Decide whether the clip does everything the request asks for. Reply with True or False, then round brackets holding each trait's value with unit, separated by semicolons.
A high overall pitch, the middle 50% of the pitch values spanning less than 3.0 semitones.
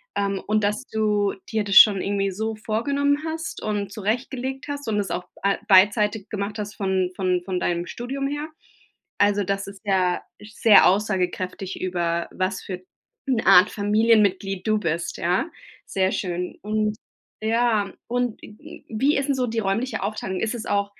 True (205 Hz; 2.6 semitones)